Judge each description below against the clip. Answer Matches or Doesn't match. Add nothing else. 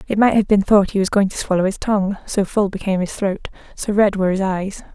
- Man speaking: Doesn't match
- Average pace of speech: Doesn't match